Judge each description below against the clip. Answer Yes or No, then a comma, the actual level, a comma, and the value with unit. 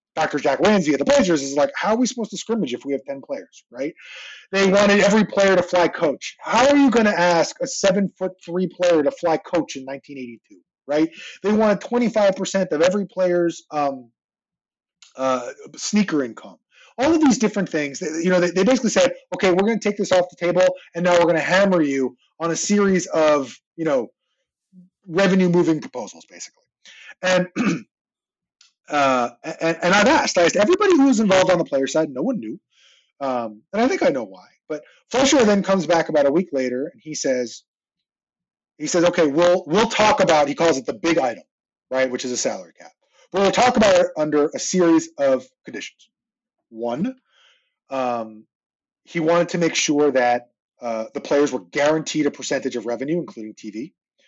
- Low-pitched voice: No, medium, 175 Hz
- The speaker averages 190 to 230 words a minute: Yes, average, 200 wpm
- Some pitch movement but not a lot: No, wide, 6.2 semitones